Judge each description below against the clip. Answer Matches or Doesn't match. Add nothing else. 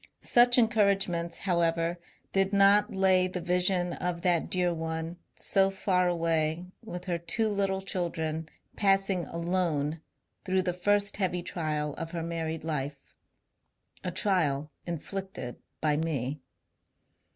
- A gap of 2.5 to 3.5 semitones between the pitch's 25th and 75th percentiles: Matches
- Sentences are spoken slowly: Matches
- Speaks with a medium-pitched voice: Matches